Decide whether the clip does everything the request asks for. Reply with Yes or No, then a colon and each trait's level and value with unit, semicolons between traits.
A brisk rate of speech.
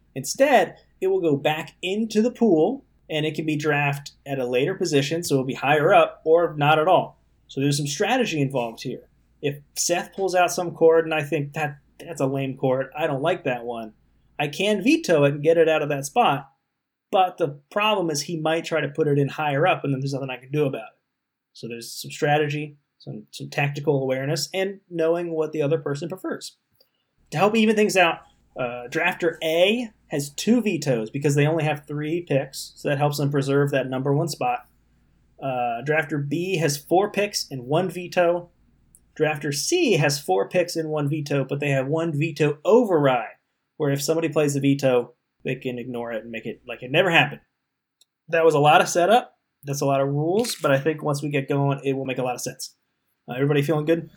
Yes: fast, 215 wpm